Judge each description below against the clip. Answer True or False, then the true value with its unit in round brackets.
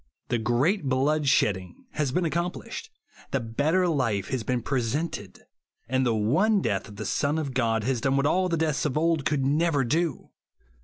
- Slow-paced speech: False (195 wpm)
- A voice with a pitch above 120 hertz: True (140 Hz)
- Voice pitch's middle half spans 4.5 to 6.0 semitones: True (5.1 semitones)